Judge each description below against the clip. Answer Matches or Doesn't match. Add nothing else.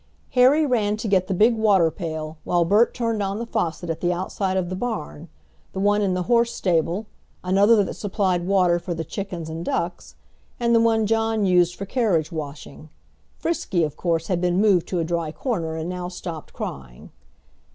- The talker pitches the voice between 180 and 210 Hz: Matches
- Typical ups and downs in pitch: Matches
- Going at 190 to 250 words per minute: Matches